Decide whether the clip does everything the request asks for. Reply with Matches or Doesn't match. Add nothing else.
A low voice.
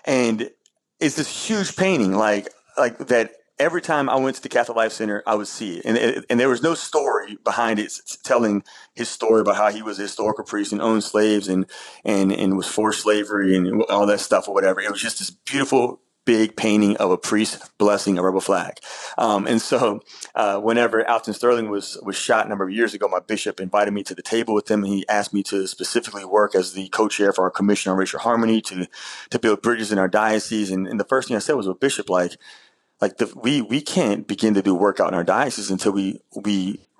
Matches